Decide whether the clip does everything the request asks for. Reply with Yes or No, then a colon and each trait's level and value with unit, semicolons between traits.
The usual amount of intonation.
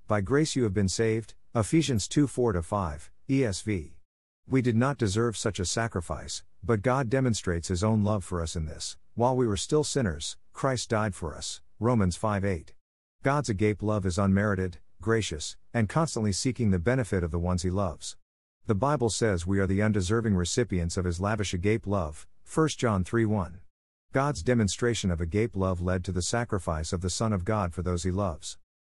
Yes: average, 4.5 semitones